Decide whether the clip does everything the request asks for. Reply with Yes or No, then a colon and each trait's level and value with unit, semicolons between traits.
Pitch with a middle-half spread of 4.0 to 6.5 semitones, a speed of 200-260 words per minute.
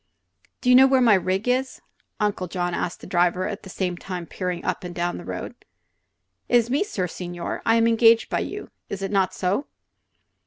Yes: average, 4.3 semitones; fast, 205 wpm